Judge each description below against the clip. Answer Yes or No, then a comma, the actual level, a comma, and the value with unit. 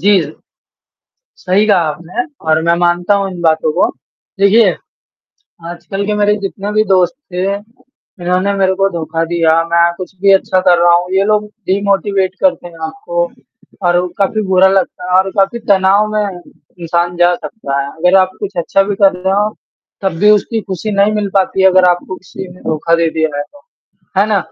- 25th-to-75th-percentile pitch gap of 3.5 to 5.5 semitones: No, narrow, 2.6 semitones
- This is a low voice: No, high, 190 Hz